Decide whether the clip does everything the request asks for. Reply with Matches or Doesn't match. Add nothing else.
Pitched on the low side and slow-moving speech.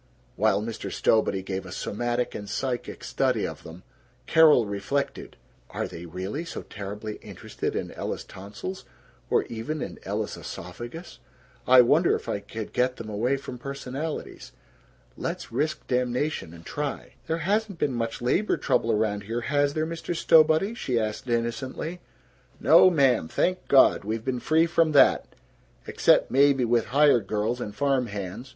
Doesn't match